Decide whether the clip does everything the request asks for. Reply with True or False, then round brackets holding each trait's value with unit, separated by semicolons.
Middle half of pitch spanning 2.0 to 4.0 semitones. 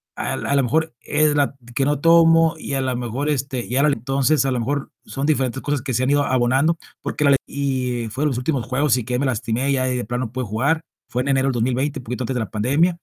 True (2.6 semitones)